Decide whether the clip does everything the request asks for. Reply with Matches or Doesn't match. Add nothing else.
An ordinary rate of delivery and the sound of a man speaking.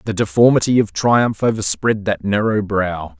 Matches